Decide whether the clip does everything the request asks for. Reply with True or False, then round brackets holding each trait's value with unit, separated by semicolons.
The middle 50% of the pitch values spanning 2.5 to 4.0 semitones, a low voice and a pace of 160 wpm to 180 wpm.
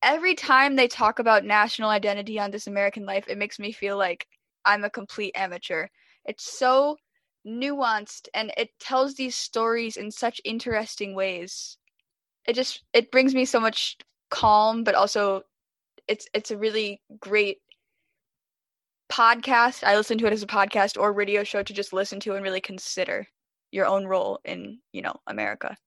False (3.4 semitones; 215 Hz; 165 wpm)